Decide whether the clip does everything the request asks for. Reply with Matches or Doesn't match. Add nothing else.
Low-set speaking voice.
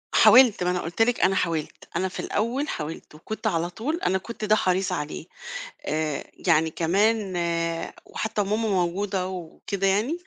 Doesn't match